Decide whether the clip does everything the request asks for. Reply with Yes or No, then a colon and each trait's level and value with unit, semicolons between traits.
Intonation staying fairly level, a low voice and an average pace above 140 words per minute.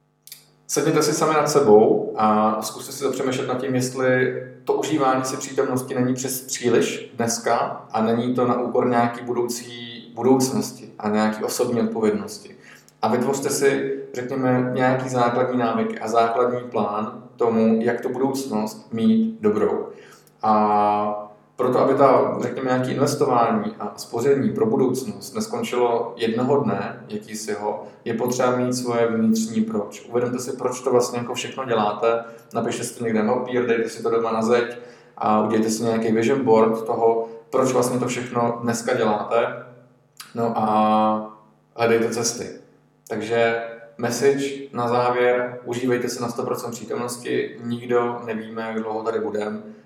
Yes: narrow, 2.1 semitones; low, 120 Hz; average, 150 wpm